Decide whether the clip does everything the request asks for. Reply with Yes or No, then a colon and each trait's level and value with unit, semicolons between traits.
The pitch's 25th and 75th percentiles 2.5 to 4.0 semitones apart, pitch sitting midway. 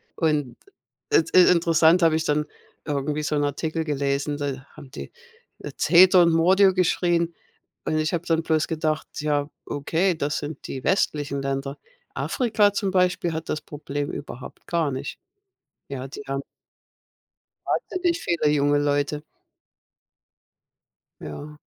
Yes: average, 2.9 semitones; medium, 155 Hz